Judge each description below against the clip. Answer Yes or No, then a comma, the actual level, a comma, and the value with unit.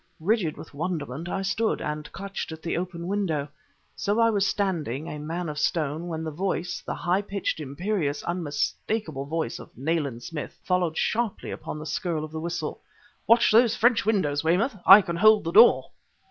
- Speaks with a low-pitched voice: No, medium, 170 Hz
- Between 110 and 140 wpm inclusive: No, average, 180 wpm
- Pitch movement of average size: Yes, average, 4.5 semitones